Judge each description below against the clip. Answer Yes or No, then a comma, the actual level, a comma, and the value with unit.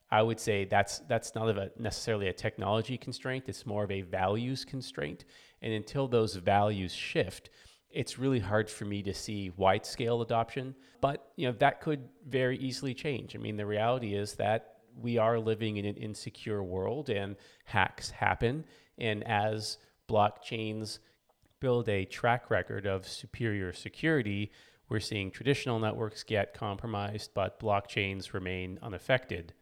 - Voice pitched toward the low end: Yes, low, 110 Hz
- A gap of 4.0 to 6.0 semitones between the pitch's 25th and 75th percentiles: No, average, 3.1 semitones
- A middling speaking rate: Yes, average, 155 wpm